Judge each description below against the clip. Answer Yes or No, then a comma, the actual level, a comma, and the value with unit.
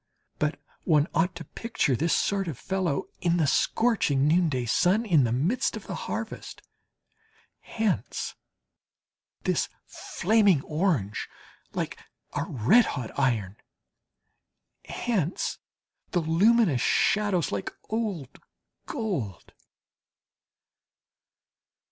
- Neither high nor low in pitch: Yes, medium, 170 Hz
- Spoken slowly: Yes, slow, 100 wpm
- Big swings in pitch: Yes, wide, 6.7 semitones